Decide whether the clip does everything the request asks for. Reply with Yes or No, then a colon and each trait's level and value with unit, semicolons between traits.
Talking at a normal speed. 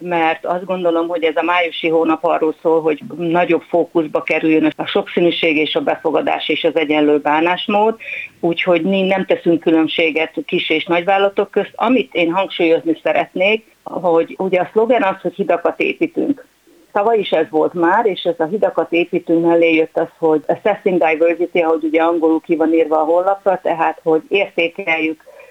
No: fast, 170 wpm